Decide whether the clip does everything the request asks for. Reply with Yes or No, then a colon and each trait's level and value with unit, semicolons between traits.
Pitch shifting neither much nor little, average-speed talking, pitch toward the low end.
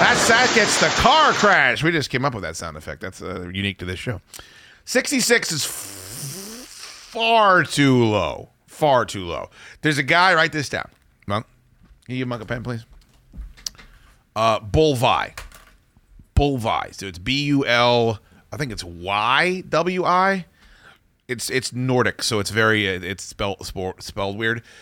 No: wide, 7.4 semitones; average, 160 wpm; low, 120 Hz